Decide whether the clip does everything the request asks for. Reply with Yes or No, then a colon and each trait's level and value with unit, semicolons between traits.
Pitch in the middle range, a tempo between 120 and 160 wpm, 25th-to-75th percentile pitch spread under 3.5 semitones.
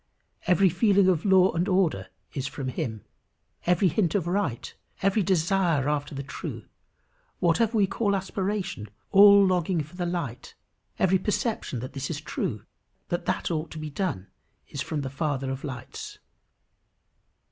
No: medium, 175 Hz; average, 155 wpm; average, 5.3 semitones